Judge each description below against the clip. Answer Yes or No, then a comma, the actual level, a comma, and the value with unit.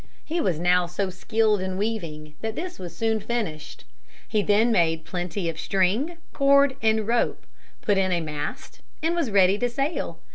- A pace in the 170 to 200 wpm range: Yes, average, 175 wpm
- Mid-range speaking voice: No, high, 205 Hz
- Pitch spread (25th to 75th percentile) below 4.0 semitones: No, average, 4.7 semitones